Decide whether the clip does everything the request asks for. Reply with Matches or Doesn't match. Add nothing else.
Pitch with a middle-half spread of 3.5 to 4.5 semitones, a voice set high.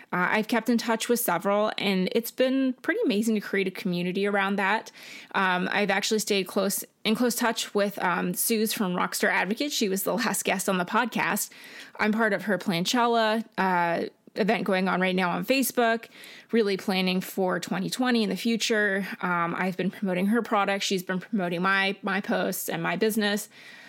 Doesn't match